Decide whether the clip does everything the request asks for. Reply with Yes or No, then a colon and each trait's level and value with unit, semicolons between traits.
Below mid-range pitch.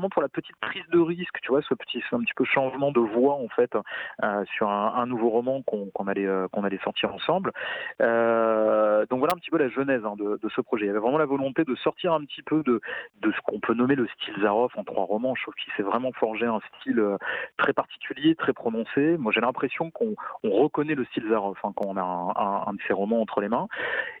Yes: low, 120 Hz